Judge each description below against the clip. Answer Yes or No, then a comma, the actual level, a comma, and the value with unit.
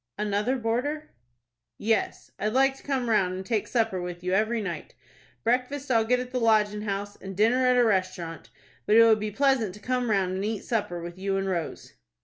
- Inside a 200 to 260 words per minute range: Yes, fast, 205 wpm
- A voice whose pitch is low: No, high, 215 Hz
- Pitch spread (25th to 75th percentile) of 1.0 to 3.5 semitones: No, average, 4.3 semitones